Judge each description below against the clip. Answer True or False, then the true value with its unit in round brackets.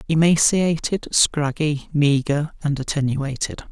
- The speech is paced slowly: True (80 wpm)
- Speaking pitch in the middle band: True (150 Hz)